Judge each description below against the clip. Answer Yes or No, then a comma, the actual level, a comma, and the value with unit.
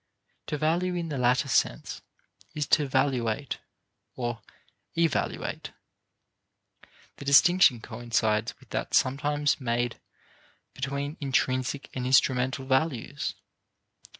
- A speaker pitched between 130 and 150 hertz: Yes, low, 135 Hz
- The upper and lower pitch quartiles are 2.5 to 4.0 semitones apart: Yes, average, 2.8 semitones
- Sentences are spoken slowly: Yes, slow, 95 wpm